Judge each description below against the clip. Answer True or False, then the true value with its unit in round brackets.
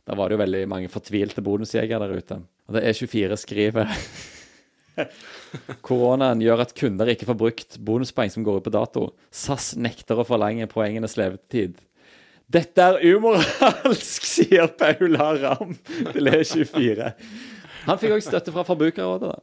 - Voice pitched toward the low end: True (115 Hz)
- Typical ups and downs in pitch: False (6.1 semitones)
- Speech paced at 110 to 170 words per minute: True (150 wpm)